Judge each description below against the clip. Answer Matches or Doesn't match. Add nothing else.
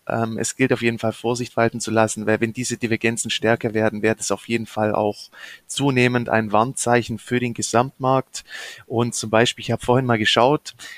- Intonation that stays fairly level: Matches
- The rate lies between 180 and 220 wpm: Matches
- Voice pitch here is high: Doesn't match